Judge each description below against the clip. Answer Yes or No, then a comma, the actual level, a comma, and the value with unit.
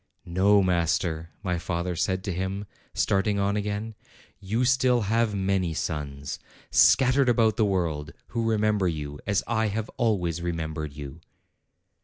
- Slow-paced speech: No, average, 145 wpm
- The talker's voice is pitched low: Yes, very low, 95 Hz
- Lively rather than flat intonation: No, average, 4.2 semitones